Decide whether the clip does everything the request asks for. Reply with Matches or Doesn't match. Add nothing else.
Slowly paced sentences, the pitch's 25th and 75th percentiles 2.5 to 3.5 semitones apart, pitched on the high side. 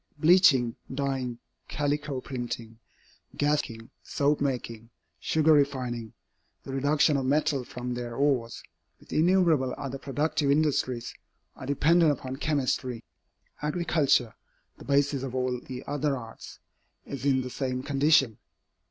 Doesn't match